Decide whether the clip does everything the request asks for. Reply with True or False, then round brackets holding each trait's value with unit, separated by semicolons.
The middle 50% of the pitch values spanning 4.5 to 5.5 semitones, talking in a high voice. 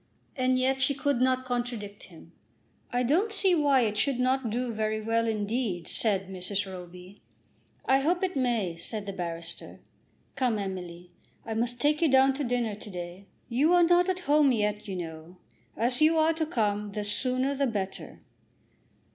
True (5.1 semitones; 235 Hz)